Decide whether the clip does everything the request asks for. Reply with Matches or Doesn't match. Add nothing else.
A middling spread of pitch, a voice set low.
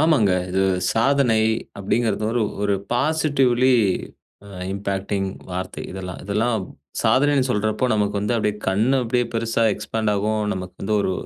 Matches